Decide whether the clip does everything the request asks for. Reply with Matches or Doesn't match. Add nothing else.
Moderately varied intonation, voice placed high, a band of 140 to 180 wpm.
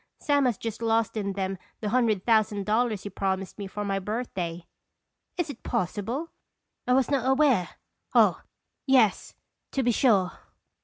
Matches